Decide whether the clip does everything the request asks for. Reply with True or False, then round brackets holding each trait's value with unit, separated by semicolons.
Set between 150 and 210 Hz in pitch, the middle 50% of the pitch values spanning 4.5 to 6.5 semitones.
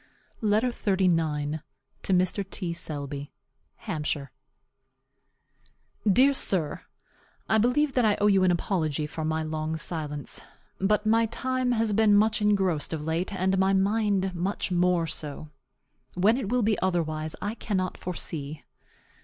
True (185 Hz; 5.0 semitones)